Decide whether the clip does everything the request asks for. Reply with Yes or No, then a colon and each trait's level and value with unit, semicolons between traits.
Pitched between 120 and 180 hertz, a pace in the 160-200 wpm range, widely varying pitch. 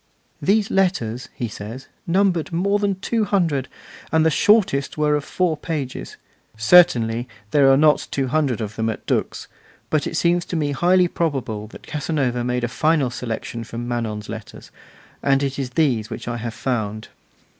Yes: medium, 140 Hz; average, 175 wpm; wide, 5.9 semitones